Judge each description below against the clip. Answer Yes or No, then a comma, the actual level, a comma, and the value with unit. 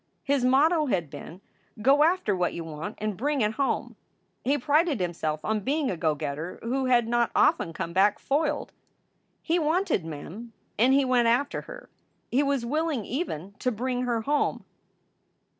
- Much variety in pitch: Yes, wide, 6.8 semitones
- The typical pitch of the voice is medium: No, high, 245 Hz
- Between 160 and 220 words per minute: Yes, average, 170 wpm